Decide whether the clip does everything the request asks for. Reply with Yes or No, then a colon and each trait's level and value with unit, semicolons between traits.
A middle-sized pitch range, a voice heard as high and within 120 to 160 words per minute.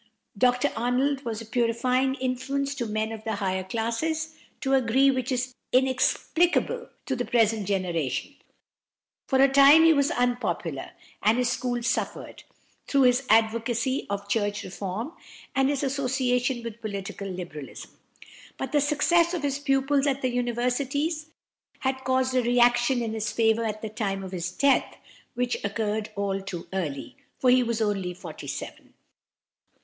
Yes: average, 3.7 semitones; high, 245 Hz; average, 155 wpm